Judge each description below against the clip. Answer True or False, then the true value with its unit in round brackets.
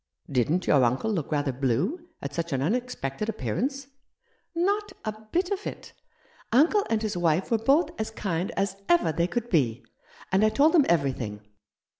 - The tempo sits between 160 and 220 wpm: True (180 wpm)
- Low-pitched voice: False (195 Hz)